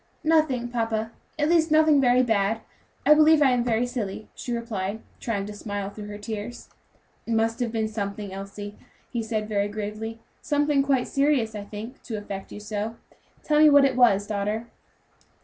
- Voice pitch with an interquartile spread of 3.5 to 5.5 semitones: Yes, average, 3.8 semitones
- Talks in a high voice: Yes, high, 225 Hz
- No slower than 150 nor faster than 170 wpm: No, average, 180 wpm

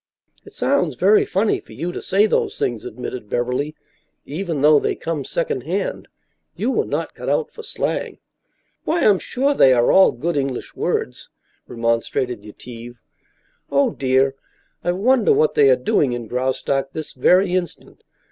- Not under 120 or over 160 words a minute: Yes, average, 155 wpm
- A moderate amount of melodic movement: No, wide, 8.1 semitones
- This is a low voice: No, medium, 150 Hz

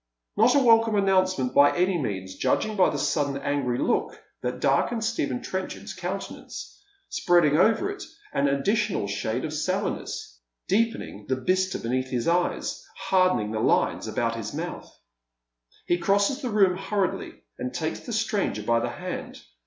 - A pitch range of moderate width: No, wide, 8.0 semitones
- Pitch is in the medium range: Yes, medium, 180 Hz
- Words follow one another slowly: No, average, 155 wpm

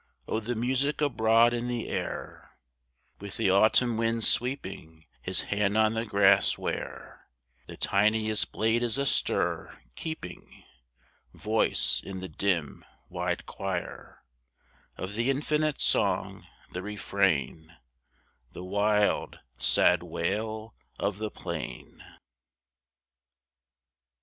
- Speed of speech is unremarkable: No, slow, 105 wpm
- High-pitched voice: No, low, 110 Hz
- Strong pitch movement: No, average, 3.2 semitones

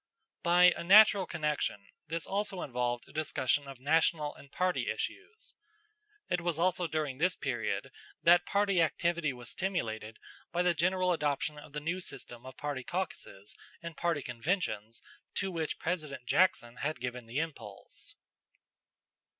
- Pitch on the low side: No, medium, 160 Hz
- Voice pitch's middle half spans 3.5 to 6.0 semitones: Yes, average, 5.1 semitones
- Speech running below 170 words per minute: Yes, average, 145 wpm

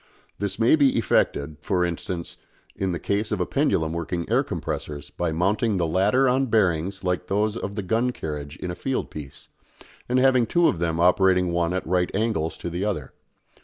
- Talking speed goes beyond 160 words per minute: Yes, average, 195 wpm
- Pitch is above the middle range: No, very low, 90 Hz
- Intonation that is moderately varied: Yes, average, 4.5 semitones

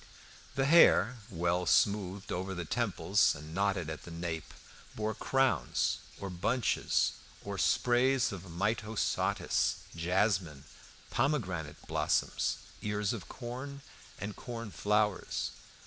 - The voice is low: Yes, low, 100 Hz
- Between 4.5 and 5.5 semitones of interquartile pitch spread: Yes, average, 5.1 semitones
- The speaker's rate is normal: No, slow, 110 wpm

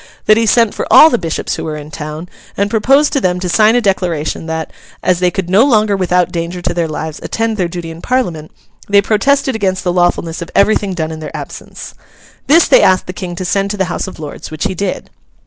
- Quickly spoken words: Yes, fast, 235 wpm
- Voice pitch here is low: No, medium, 185 Hz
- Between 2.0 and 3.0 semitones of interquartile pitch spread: No, average, 4.2 semitones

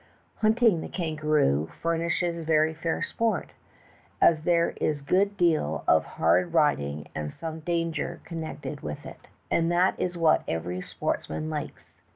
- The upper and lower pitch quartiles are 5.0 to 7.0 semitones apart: No, narrow, 2.5 semitones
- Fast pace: No, average, 150 wpm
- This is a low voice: No, medium, 160 Hz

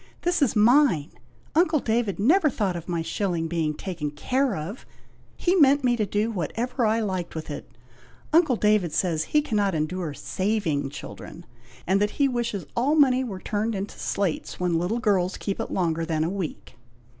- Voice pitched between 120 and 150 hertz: No, high, 205 Hz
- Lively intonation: Yes, wide, 6.1 semitones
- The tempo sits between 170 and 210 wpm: Yes, average, 180 wpm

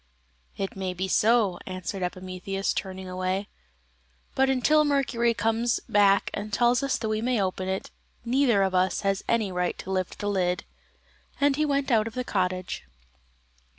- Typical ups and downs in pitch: Yes, average, 4.3 semitones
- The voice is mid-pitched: No, high, 200 Hz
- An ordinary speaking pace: Yes, average, 165 wpm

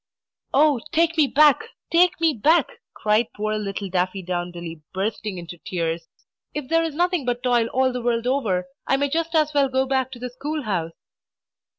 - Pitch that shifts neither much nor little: No, wide, 7.2 semitones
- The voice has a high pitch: Yes, very high, 250 Hz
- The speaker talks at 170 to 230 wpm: Yes, average, 180 wpm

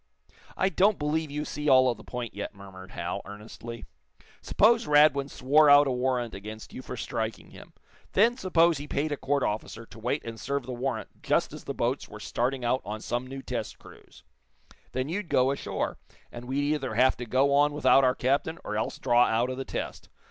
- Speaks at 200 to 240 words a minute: Yes, fast, 205 wpm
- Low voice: Yes, low, 130 Hz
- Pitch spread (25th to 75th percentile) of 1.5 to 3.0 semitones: No, average, 3.8 semitones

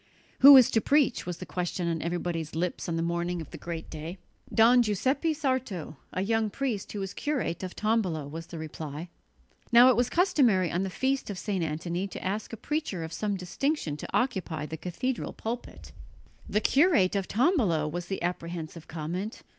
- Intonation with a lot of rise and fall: Yes, wide, 6.2 semitones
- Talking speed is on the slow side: No, average, 185 wpm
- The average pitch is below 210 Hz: Yes, medium, 185 Hz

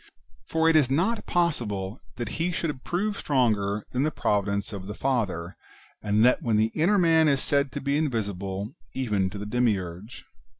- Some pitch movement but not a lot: No, wide, 7.0 semitones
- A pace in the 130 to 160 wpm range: No, average, 175 wpm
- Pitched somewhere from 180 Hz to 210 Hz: No, low, 120 Hz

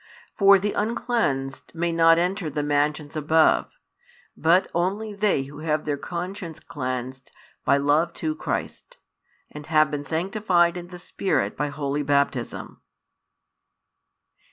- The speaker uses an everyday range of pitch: Yes, average, 3.7 semitones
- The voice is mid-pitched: Yes, medium, 160 Hz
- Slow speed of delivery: Yes, slow, 130 wpm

